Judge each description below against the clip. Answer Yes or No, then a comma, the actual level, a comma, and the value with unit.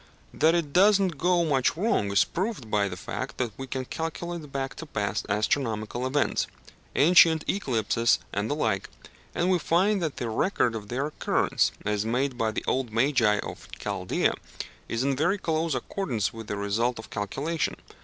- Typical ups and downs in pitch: No, wide, 6.8 semitones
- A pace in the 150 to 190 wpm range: Yes, average, 175 wpm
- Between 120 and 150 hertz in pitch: Yes, low, 135 Hz